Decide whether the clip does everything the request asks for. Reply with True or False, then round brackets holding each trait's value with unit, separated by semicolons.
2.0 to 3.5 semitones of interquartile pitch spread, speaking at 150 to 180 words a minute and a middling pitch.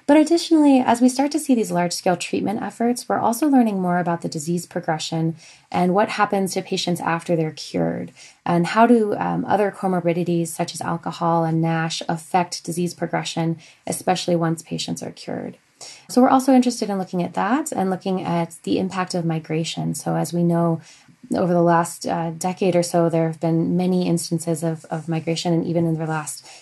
False (2.8 semitones; 195 wpm; 175 Hz)